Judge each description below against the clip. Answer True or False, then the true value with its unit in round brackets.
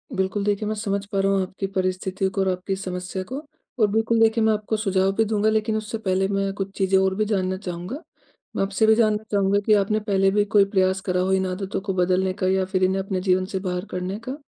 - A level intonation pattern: True (2.0 semitones)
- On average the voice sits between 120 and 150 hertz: False (195 Hz)